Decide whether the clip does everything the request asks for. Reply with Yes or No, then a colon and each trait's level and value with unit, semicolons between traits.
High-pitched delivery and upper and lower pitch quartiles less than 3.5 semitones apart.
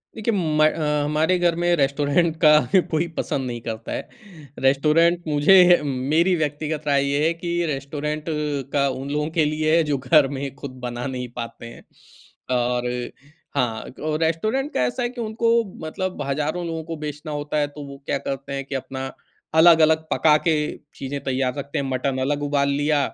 No: medium, 150 Hz; average, 3.1 semitones